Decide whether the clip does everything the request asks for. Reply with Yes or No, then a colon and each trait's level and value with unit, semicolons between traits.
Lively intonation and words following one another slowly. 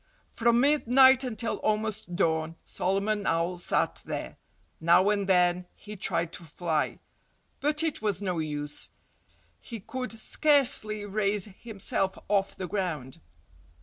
No: average, 4.3 semitones; slow, 125 wpm